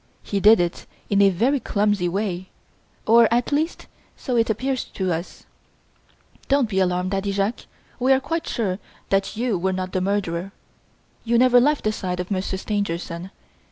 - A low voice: No, high, 200 Hz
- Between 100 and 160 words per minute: No, average, 170 wpm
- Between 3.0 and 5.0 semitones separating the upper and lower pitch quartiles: Yes, average, 4.1 semitones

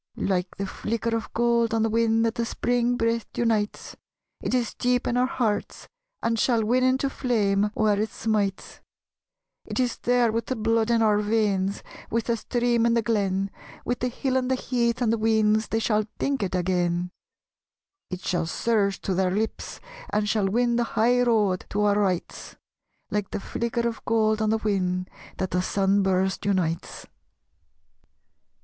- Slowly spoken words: No, average, 175 wpm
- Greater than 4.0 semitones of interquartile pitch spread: No, average, 2.9 semitones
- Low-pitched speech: No, high, 220 Hz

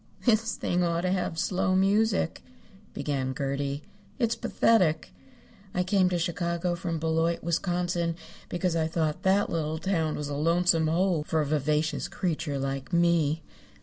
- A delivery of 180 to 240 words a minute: No, average, 150 wpm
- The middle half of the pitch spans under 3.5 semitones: Yes, average, 2.7 semitones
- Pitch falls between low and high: Yes, medium, 170 Hz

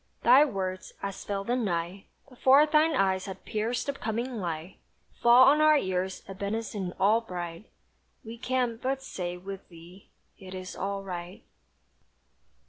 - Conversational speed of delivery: Yes, average, 150 wpm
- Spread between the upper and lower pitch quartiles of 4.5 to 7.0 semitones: Yes, average, 4.8 semitones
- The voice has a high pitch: Yes, high, 200 Hz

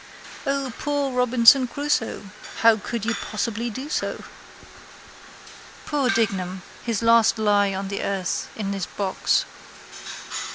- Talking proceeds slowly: Yes, slow, 120 wpm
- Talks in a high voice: Yes, high, 230 Hz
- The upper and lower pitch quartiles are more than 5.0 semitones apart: No, average, 4.0 semitones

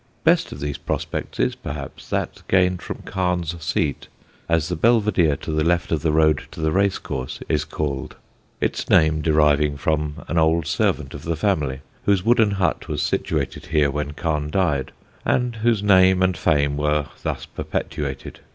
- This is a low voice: Yes, very low, 80 Hz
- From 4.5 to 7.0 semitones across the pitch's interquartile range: No, average, 3.7 semitones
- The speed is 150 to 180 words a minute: Yes, average, 170 wpm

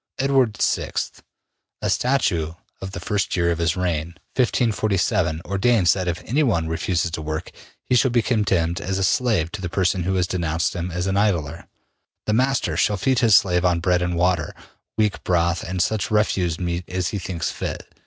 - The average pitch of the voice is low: Yes, very low, 90 Hz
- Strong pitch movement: No, average, 3.7 semitones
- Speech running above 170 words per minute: Yes, average, 185 wpm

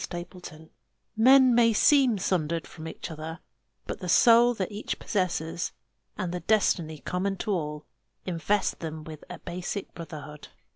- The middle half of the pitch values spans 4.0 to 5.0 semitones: Yes, average, 4.6 semitones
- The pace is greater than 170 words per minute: No, average, 155 wpm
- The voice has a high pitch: No, medium, 180 Hz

